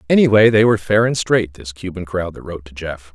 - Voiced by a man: Yes, male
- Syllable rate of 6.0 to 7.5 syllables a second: Yes, 6.1 syllables/s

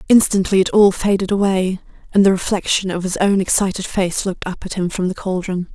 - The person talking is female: Yes, female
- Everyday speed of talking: No, fast, 210 wpm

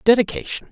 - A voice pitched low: No, high, 230 Hz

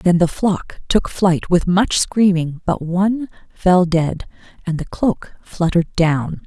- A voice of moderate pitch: Yes, medium, 180 Hz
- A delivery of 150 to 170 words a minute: Yes, average, 160 wpm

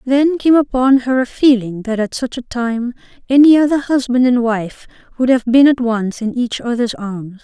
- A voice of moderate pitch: No, high, 245 Hz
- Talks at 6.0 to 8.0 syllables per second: No, 4.7 syllables/s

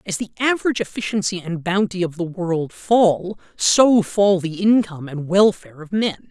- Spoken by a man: Yes, male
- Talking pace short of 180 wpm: Yes, average, 170 wpm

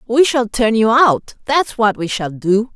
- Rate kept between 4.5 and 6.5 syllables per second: No, 4.0 syllables/s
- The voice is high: Yes, high, 230 Hz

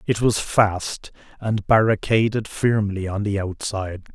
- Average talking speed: No, slow, 130 wpm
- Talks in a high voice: No, low, 105 Hz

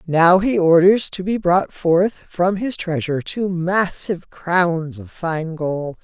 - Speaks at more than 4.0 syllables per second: No, 3.6 syllables/s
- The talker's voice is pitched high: No, medium, 175 Hz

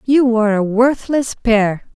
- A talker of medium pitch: No, high, 230 Hz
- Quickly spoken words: No, average, 150 wpm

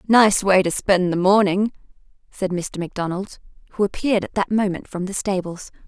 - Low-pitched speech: No, high, 190 Hz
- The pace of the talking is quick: No, average, 175 wpm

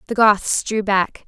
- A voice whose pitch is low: No, high, 205 Hz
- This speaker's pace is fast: No, average, 190 wpm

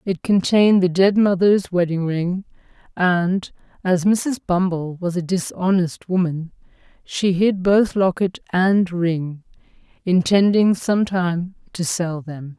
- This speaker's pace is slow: Yes, slow, 125 wpm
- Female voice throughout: Yes, female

